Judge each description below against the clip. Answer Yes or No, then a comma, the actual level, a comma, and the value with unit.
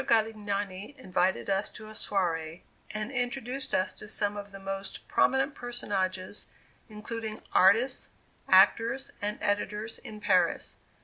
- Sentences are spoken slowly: Yes, slow, 125 wpm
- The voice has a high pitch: Yes, high, 210 Hz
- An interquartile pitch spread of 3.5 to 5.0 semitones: No, average, 2.8 semitones